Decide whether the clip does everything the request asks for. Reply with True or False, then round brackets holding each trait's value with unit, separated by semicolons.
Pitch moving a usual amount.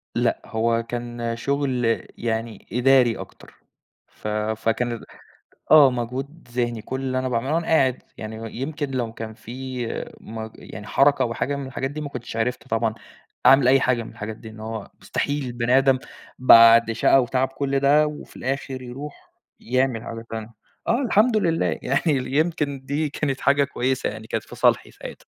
True (3.2 semitones)